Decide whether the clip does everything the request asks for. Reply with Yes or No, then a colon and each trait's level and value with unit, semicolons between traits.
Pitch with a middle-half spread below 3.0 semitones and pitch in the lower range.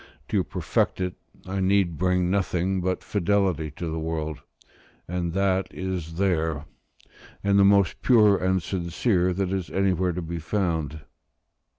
Yes: narrow, 2.6 semitones; very low, 90 Hz